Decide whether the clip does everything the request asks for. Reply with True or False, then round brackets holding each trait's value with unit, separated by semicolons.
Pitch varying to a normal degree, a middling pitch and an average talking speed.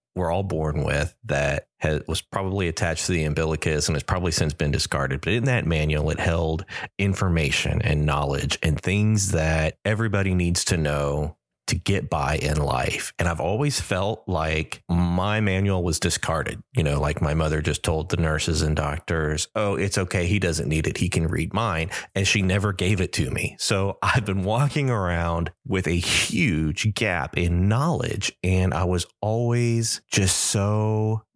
False (4.2 semitones; 90 Hz; 180 wpm)